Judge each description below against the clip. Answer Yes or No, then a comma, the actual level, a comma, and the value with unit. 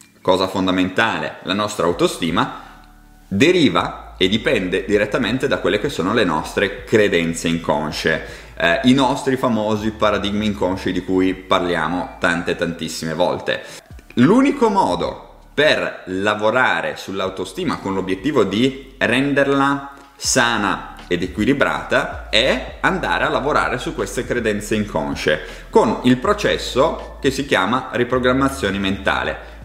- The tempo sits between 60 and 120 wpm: Yes, slow, 115 wpm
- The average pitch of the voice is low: Yes, low, 100 Hz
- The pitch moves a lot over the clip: Yes, wide, 6.1 semitones